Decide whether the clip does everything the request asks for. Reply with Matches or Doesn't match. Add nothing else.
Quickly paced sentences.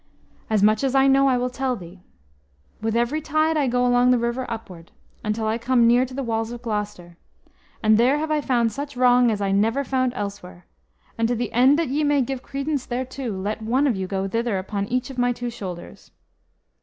Matches